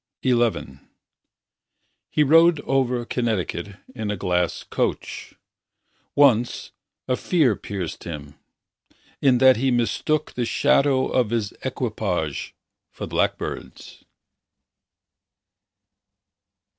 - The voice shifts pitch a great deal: No, average, 4.6 semitones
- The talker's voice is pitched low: Yes, low, 120 Hz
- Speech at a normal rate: No, slow, 90 wpm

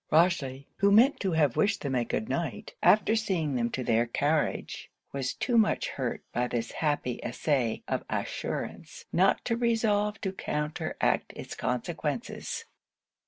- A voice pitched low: No, medium, 155 Hz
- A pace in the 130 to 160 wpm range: Yes, average, 150 wpm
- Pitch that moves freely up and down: Yes, wide, 7.9 semitones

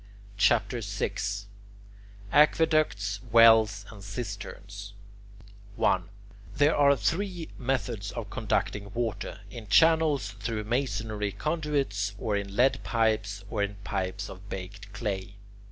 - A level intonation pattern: No, average, 4.2 semitones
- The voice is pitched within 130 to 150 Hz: No, low, 110 Hz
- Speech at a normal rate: No, slow, 110 wpm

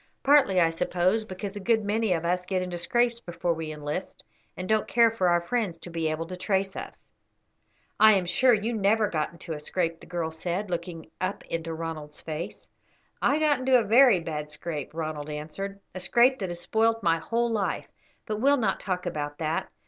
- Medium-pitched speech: Yes, medium, 180 Hz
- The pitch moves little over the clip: No, average, 4.8 semitones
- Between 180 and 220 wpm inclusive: Yes, fast, 205 wpm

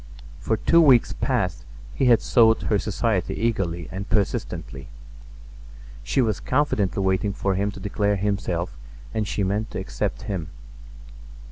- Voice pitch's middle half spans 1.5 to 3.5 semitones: Yes, average, 2.8 semitones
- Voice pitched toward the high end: No, low, 100 Hz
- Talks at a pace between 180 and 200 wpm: No, average, 140 wpm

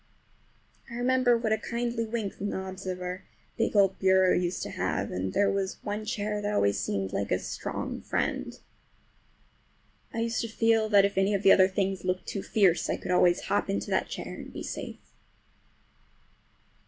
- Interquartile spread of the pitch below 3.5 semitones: Yes, average, 3.0 semitones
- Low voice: No, high, 195 Hz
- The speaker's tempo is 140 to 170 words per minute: No, average, 185 wpm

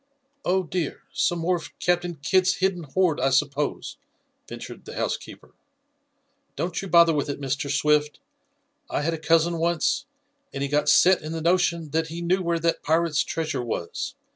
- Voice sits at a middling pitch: Yes, medium, 165 Hz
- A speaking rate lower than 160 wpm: No, average, 170 wpm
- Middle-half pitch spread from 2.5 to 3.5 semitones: Yes, average, 2.9 semitones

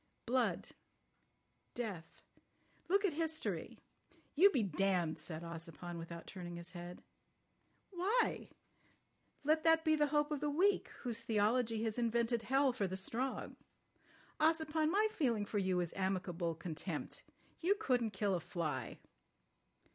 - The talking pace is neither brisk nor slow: No, slow, 130 wpm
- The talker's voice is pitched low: No, high, 230 Hz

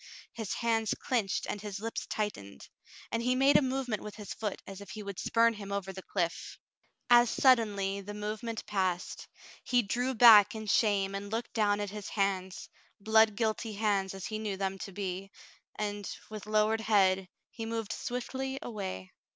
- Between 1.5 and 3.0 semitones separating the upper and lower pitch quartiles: Yes, narrow, 2.5 semitones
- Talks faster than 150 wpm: Yes, average, 175 wpm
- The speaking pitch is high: Yes, high, 210 Hz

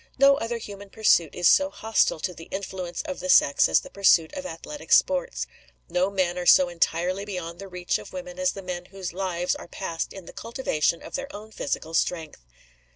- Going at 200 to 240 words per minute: Yes, fast, 205 wpm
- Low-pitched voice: No, high, 190 Hz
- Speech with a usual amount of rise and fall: Yes, average, 4.6 semitones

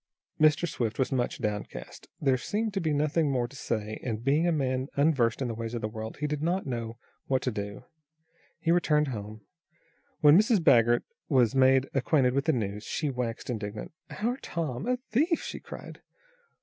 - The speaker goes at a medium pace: Yes, average, 190 wpm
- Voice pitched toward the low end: Yes, low, 130 Hz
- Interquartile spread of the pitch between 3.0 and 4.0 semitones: No, average, 5.1 semitones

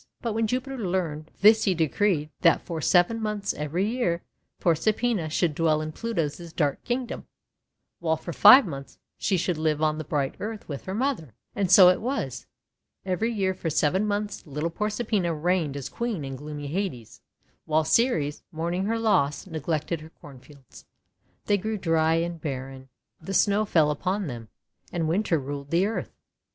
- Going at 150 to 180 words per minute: Yes, average, 165 wpm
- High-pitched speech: No, medium, 170 Hz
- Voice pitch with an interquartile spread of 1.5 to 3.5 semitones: No, average, 5.3 semitones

